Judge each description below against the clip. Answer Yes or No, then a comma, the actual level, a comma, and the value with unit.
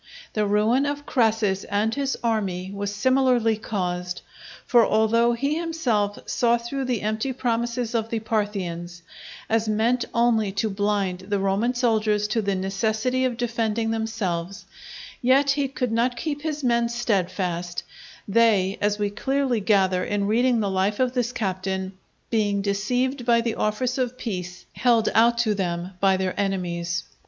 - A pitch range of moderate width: Yes, average, 3.5 semitones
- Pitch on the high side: Yes, high, 220 Hz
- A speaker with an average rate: Yes, average, 155 wpm